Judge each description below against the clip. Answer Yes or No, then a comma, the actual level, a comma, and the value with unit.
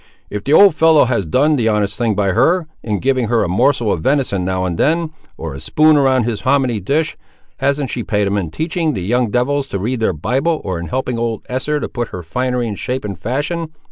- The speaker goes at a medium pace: No, fast, 235 wpm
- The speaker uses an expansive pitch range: Yes, wide, 5.8 semitones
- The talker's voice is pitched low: Yes, low, 125 Hz